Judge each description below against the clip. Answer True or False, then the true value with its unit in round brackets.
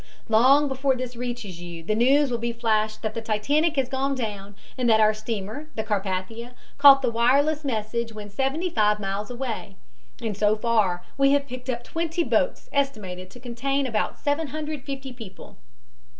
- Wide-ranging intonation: False (4.3 semitones)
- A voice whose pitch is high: True (235 Hz)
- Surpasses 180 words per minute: False (170 wpm)